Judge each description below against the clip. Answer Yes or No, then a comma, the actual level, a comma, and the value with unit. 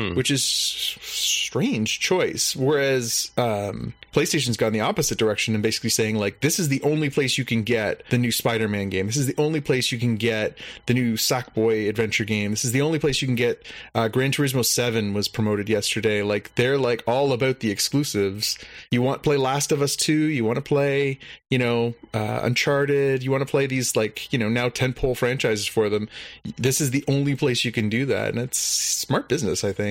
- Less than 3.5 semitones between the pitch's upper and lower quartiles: No, average, 3.9 semitones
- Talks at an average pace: No, fast, 215 wpm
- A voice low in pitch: Yes, low, 120 Hz